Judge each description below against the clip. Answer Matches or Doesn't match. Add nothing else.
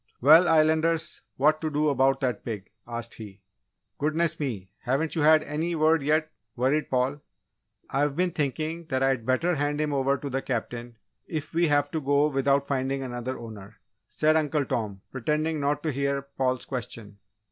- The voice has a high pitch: Doesn't match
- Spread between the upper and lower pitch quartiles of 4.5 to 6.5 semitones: Doesn't match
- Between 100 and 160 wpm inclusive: Doesn't match